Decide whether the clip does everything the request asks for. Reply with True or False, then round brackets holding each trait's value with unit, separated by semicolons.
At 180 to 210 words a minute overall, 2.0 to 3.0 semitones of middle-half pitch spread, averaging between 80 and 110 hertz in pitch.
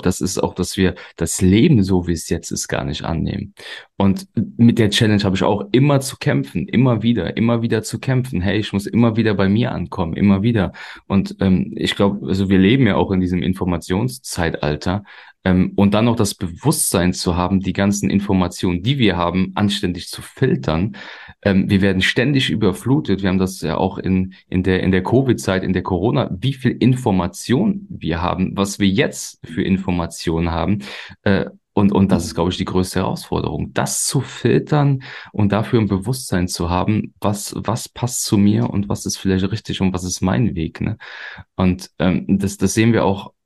False (190 wpm; 3.5 semitones; 95 Hz)